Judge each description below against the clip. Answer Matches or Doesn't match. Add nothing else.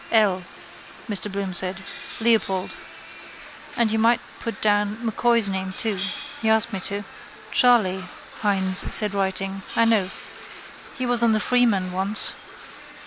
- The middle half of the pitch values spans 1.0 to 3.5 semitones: Matches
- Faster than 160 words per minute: Doesn't match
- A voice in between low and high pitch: Doesn't match